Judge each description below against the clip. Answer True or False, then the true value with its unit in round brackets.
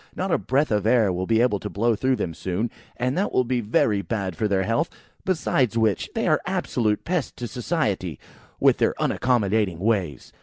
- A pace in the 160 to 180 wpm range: False (195 wpm)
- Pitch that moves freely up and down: False (4.2 semitones)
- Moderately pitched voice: False (110 Hz)